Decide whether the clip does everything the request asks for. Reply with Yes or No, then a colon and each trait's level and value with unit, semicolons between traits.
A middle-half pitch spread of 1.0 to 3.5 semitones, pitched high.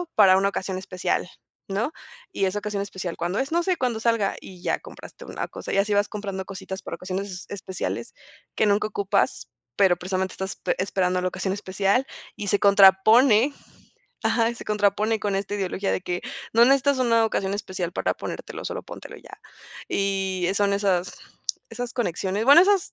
Yes: narrow, 2.6 semitones; high, 200 Hz